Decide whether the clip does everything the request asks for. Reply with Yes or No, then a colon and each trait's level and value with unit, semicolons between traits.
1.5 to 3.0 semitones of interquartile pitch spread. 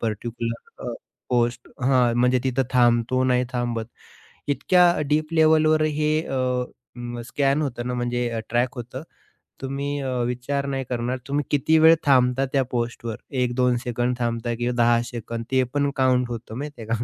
Yes: narrow, 2.5 semitones